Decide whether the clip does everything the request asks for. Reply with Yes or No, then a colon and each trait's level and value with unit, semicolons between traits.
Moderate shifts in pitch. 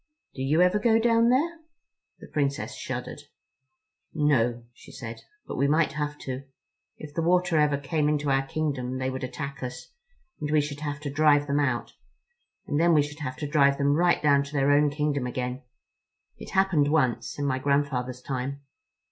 No: narrow, 2.1 semitones